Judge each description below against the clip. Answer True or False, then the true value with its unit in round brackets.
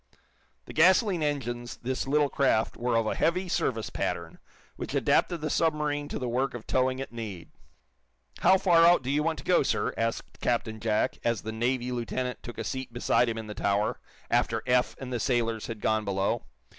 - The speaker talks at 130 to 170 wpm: False (195 wpm)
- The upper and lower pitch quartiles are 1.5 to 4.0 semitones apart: False (4.4 semitones)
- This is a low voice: True (125 Hz)